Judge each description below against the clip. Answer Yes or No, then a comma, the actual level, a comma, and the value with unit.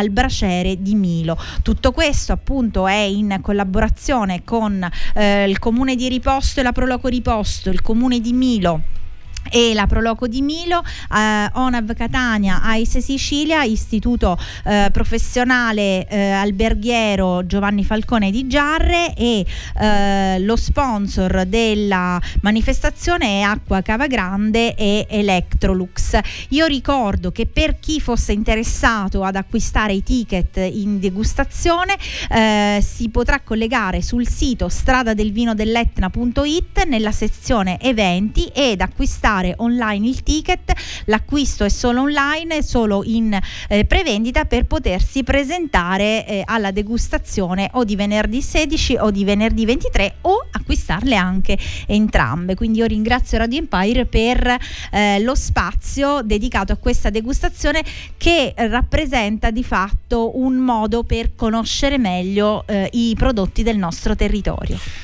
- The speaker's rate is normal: Yes, average, 125 wpm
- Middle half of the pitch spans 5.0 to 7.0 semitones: No, average, 4.0 semitones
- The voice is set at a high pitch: Yes, high, 225 Hz